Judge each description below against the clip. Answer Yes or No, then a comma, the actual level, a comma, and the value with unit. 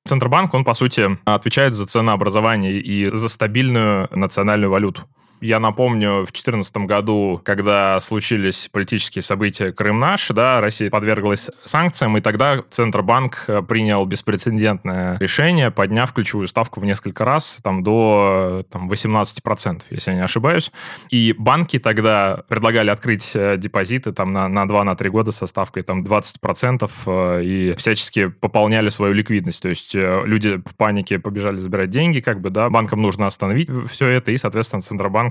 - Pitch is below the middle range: Yes, low, 105 Hz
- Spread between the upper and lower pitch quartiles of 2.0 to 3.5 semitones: Yes, narrow, 2.6 semitones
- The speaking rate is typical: Yes, average, 150 wpm